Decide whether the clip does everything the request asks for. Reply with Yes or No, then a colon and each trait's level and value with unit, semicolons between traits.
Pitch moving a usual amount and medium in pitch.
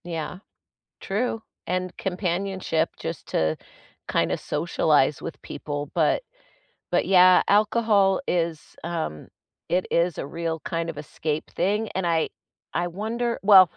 Yes: average, 3.2 semitones; medium, 175 Hz